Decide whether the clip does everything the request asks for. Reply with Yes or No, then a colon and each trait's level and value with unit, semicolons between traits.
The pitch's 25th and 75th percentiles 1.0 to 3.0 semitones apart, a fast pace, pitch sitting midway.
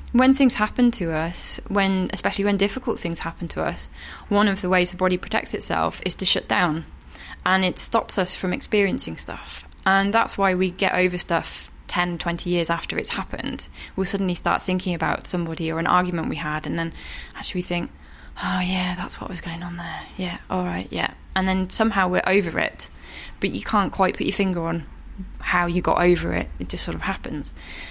Yes: narrow, 2.6 semitones; fast, 210 wpm; medium, 180 Hz